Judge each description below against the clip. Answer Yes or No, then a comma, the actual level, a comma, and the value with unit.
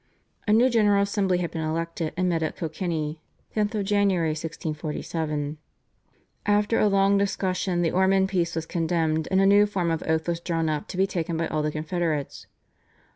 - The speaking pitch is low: No, medium, 170 Hz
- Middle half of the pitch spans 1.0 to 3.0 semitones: No, average, 3.5 semitones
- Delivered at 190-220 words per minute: No, average, 180 wpm